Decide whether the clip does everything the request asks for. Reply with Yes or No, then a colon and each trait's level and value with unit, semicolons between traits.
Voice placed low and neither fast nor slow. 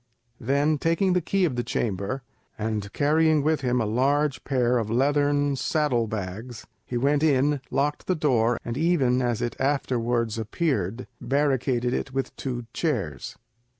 Yes: low, 130 Hz; average, 150 wpm